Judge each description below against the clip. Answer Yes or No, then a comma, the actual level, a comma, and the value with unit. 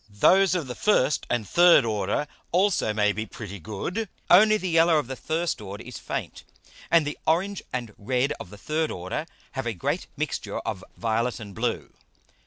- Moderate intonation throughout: No, wide, 8.4 semitones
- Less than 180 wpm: No, average, 185 wpm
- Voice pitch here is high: No, low, 130 Hz